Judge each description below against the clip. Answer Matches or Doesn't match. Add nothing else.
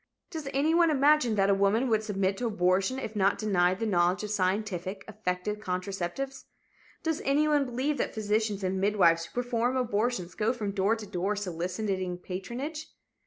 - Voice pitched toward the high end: Matches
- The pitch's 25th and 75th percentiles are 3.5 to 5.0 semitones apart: Matches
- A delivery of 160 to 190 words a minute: Matches